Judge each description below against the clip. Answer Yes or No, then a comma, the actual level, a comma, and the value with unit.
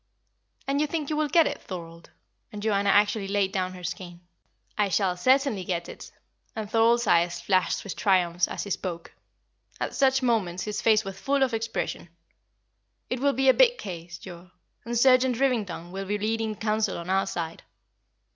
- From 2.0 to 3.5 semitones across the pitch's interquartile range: No, average, 4.9 semitones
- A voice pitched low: No, high, 205 Hz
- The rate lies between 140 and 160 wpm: No, average, 180 wpm